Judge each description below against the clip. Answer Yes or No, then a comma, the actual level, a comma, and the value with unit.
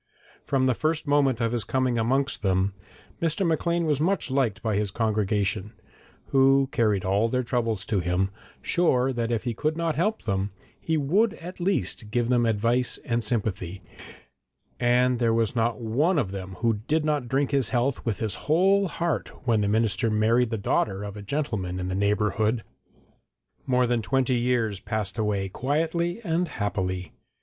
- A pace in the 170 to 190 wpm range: Yes, average, 175 wpm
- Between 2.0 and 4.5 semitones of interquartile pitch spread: No, average, 5.0 semitones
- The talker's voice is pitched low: Yes, low, 120 Hz